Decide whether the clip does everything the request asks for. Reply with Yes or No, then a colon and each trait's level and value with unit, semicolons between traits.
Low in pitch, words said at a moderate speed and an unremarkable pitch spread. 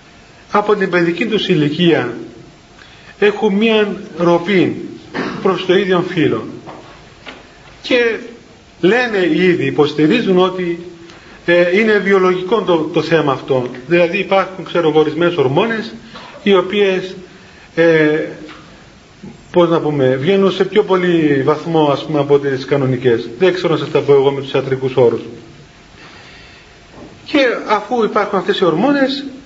No: medium, 180 Hz; average, 125 wpm; average, 4.5 semitones